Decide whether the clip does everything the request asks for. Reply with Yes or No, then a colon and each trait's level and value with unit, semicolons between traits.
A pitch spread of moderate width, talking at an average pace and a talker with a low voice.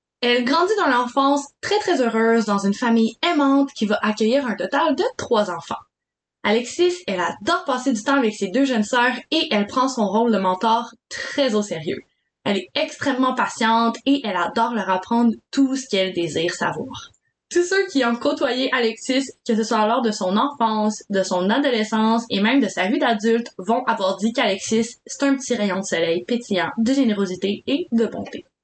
No: average, 4.2 semitones; average, 195 wpm; high, 235 Hz